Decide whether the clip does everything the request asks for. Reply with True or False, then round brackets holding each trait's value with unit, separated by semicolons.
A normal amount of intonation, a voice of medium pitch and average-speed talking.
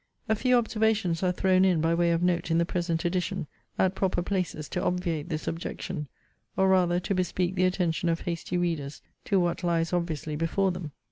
False (2.0 semitones; 175 Hz; 195 wpm)